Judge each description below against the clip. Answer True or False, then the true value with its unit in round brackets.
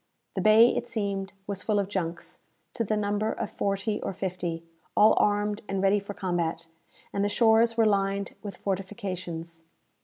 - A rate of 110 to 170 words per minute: True (165 wpm)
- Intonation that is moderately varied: False (2.1 semitones)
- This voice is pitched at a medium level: False (200 Hz)